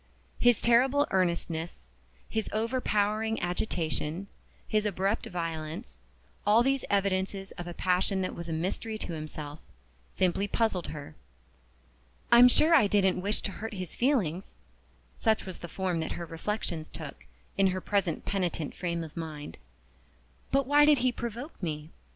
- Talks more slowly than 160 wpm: Yes, average, 145 wpm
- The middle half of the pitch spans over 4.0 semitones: Yes, average, 4.7 semitones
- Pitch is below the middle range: No, high, 190 Hz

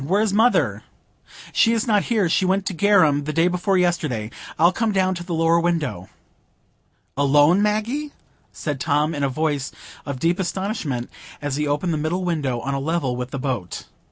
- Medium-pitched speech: Yes, medium, 165 Hz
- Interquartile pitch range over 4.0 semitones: Yes, average, 5.0 semitones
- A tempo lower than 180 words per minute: No, average, 185 wpm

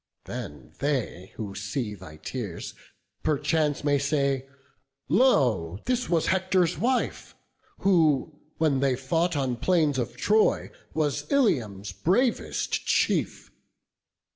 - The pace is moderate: No, slow, 110 wpm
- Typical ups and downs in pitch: No, wide, 6.2 semitones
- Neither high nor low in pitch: Yes, medium, 145 Hz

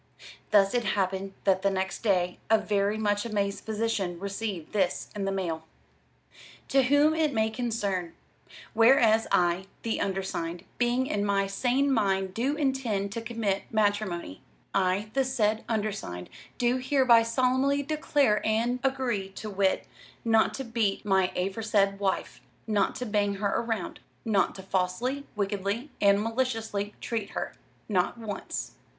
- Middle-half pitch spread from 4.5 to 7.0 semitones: No, average, 3.3 semitones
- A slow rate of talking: No, average, 145 wpm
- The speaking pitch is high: Yes, high, 210 Hz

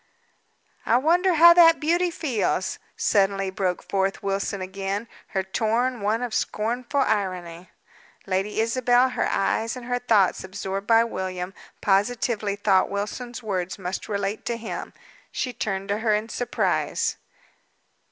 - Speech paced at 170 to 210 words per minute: No, slow, 135 wpm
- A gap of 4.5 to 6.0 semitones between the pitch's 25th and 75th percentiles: No, average, 4.0 semitones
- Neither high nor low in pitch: No, high, 210 Hz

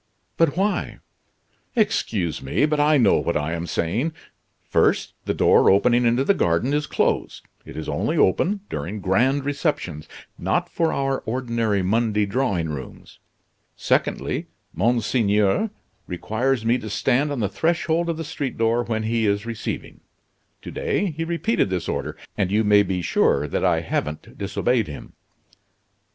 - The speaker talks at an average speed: Yes, average, 155 wpm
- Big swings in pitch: Yes, wide, 6.5 semitones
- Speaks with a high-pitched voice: No, low, 115 Hz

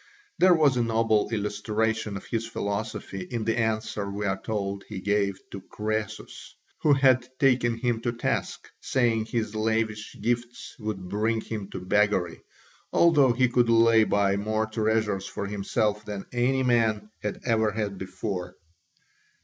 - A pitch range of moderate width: No, narrow, 2.2 semitones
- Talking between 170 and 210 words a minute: No, average, 150 wpm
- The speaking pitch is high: No, low, 110 Hz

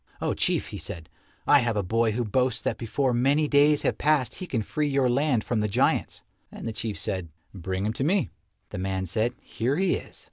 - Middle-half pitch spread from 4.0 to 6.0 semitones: Yes, average, 5.2 semitones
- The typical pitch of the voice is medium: No, low, 120 Hz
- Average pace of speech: No, fast, 220 wpm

